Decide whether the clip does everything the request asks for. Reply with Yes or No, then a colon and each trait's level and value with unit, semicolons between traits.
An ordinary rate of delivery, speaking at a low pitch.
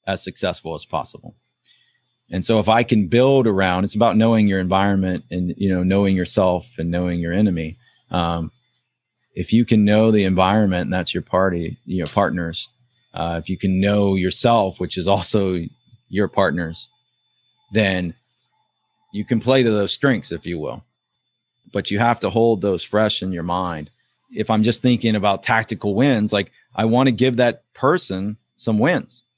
Yes: average, 175 wpm; low, 105 Hz